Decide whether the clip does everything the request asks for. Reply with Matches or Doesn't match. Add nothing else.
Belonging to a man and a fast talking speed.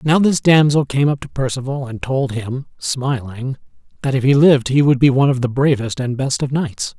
Matches